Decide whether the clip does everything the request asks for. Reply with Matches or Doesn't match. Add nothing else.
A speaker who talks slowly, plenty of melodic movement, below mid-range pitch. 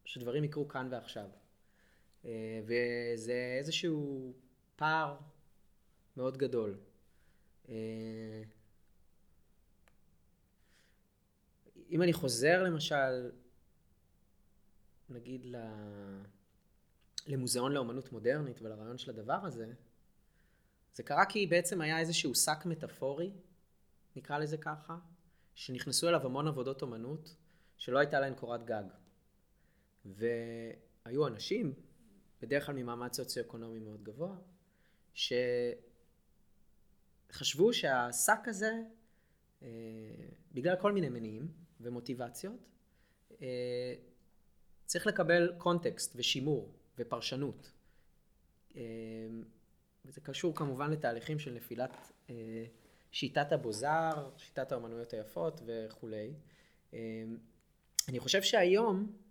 Matches